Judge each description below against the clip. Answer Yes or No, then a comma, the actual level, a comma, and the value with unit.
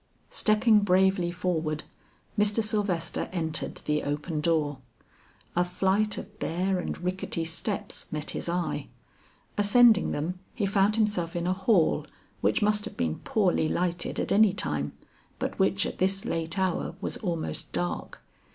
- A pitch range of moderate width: Yes, average, 3.7 semitones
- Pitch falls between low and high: Yes, medium, 180 Hz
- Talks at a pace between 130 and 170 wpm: Yes, average, 145 wpm